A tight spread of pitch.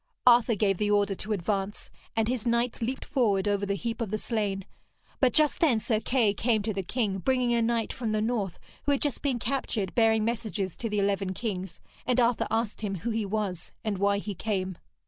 No: average, 3.0 semitones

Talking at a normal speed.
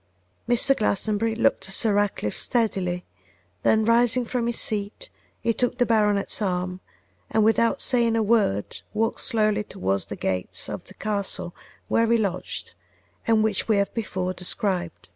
Yes: average, 155 wpm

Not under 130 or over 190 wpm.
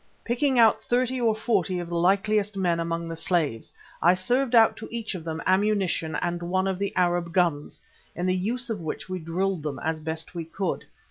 No: fast, 205 wpm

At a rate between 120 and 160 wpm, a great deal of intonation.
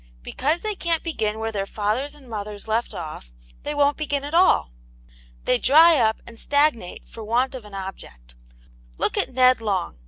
No: average, 180 wpm; wide, 5.7 semitones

